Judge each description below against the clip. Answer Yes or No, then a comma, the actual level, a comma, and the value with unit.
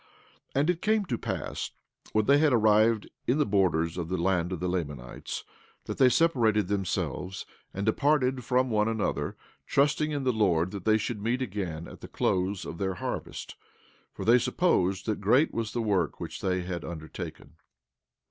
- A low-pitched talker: Yes, low, 105 Hz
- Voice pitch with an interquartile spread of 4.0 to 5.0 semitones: No, wide, 5.5 semitones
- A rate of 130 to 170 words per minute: No, average, 180 wpm